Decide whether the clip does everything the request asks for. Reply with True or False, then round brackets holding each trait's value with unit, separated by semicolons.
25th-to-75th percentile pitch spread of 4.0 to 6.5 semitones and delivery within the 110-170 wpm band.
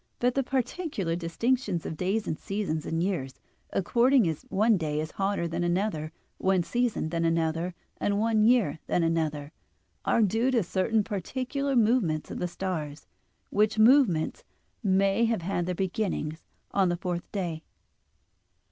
True (5.2 semitones; 150 wpm)